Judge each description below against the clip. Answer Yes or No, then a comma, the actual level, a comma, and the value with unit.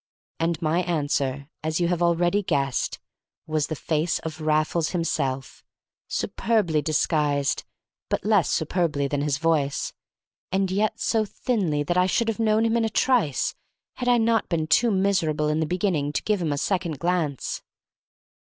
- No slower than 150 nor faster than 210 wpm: Yes, average, 160 wpm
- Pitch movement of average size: Yes, average, 4.5 semitones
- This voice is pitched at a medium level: Yes, medium, 165 Hz